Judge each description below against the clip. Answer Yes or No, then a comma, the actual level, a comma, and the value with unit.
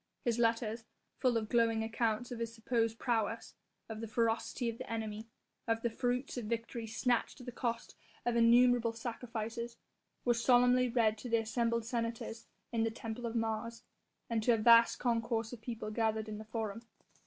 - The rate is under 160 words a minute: No, average, 175 wpm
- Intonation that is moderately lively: No, narrow, 1.2 semitones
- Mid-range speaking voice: No, high, 230 Hz